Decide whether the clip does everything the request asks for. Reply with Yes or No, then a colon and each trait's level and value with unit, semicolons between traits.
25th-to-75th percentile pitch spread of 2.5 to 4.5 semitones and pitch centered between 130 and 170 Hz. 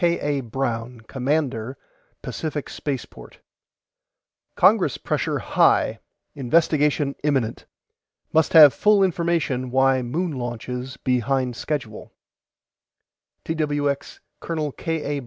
Yes: average, 3.7 semitones; medium, 140 Hz